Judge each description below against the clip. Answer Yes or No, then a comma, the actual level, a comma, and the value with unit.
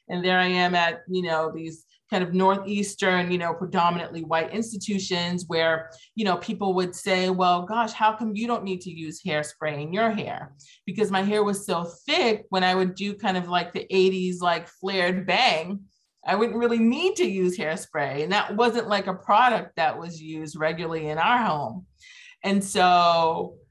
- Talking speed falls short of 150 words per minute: No, average, 190 wpm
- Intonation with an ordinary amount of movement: Yes, average, 3.3 semitones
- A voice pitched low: No, medium, 185 Hz